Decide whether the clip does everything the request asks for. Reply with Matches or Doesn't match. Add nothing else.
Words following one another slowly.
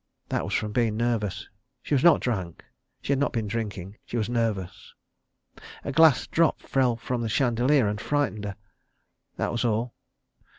Doesn't match